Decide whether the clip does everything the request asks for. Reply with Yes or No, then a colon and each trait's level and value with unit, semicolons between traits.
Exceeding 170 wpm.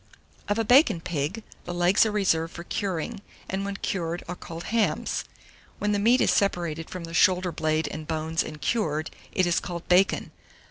Yes: average, 185 wpm